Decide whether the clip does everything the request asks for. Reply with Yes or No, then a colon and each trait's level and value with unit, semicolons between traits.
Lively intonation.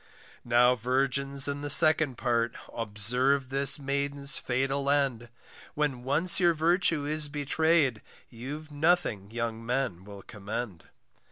No: average, 3.5 semitones